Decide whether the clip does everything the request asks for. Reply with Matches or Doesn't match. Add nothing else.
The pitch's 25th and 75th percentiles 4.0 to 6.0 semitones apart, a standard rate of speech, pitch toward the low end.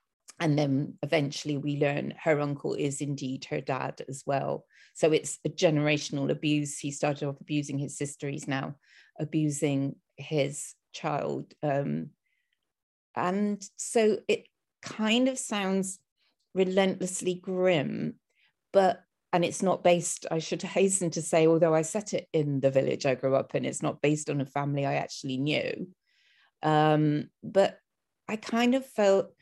Doesn't match